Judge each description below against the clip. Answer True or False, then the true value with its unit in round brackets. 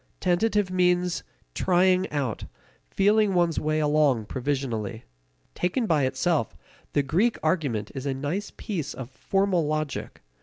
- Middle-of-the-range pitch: True (155 Hz)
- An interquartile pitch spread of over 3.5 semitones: True (5.2 semitones)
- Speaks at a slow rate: True (125 wpm)